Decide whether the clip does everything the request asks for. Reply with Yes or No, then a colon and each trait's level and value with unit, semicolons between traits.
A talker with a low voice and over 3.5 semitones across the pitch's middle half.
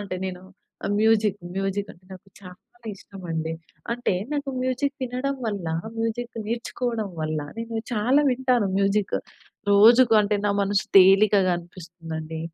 No: high, 205 Hz; average, 4.1 semitones